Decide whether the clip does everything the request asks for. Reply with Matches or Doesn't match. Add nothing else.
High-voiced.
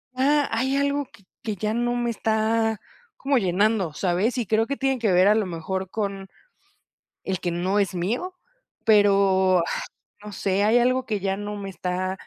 Matches